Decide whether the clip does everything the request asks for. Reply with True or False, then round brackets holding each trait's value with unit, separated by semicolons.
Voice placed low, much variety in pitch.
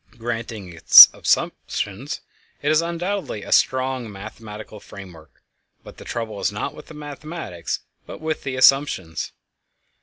True (120 Hz; 6.3 semitones)